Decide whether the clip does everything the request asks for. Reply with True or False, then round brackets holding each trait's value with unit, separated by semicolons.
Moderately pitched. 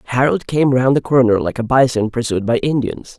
False (125 Hz)